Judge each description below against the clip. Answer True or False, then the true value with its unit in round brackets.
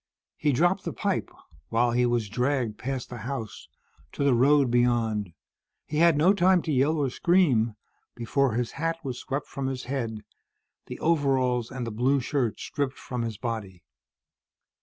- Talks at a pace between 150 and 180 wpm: True (165 wpm)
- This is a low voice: True (130 Hz)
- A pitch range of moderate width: True (3.6 semitones)